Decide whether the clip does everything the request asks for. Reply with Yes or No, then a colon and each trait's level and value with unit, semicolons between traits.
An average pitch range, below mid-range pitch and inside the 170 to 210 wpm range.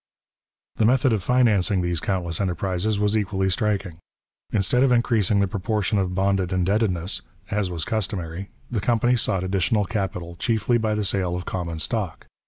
No: average, 3.1 semitones; low, 100 Hz; average, 160 wpm